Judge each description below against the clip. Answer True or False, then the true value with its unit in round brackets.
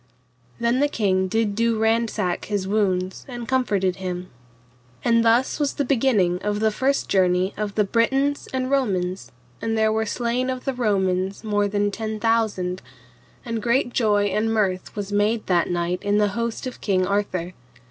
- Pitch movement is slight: False (3.5 semitones)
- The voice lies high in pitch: True (210 Hz)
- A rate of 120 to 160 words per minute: False (170 wpm)